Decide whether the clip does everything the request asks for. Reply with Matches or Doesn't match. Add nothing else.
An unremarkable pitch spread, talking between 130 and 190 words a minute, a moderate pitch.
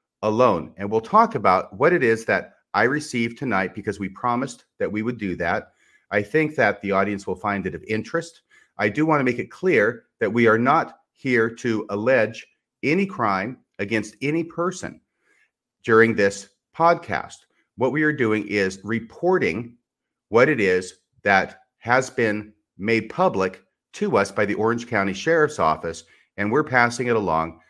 Doesn't match